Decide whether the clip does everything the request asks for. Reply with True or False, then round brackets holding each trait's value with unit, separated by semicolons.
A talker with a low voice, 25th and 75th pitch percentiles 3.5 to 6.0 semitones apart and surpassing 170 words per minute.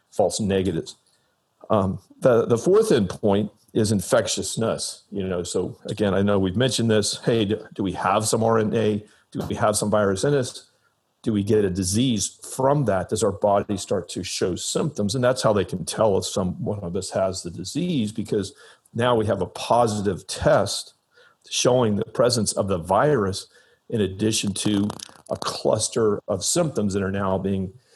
False (105 Hz; 2.9 semitones; 180 wpm)